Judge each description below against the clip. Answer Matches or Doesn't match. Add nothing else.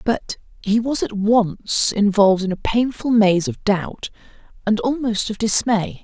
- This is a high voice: Matches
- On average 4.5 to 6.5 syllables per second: Doesn't match